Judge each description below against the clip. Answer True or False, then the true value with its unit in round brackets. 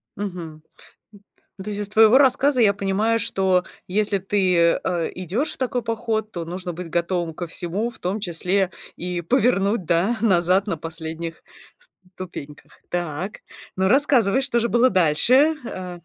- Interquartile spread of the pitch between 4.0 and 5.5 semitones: True (4.4 semitones)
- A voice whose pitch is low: False (190 Hz)